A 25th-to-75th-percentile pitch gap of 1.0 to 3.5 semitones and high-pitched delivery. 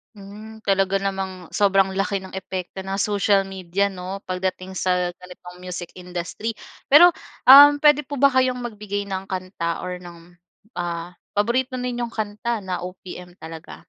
Yes: average, 2.8 semitones; high, 195 Hz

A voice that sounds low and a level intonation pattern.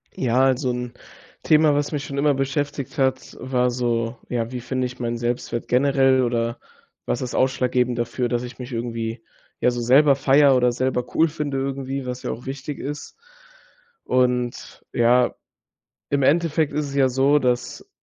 Yes: low, 130 Hz; narrow, 2.2 semitones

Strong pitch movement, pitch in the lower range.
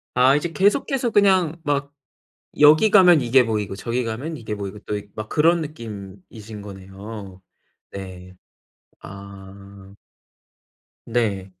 Yes: wide, 7.2 semitones; low, 110 Hz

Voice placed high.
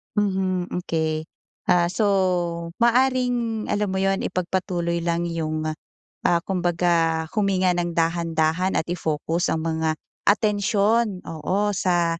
No: medium, 175 Hz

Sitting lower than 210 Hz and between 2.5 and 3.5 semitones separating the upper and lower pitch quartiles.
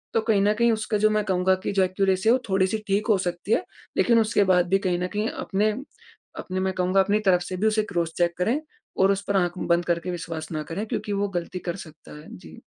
Yes: high, 190 Hz; average, 3.1 semitones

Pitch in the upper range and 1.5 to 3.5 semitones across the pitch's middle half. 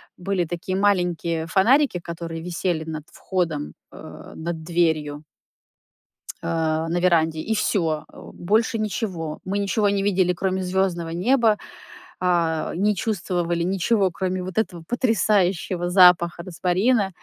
No: medium, 180 Hz; average, 2.9 semitones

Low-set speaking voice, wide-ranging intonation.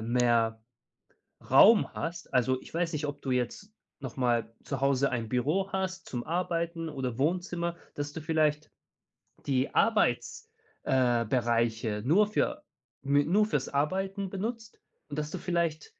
No: medium, 150 Hz; wide, 6.2 semitones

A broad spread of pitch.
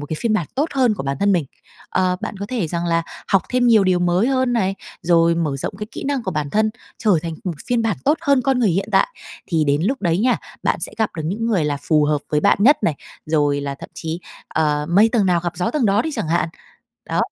Yes: wide, 6.1 semitones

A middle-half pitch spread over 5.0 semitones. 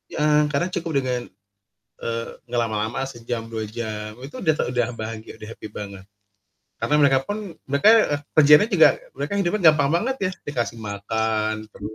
Yes: wide, 5.4 semitones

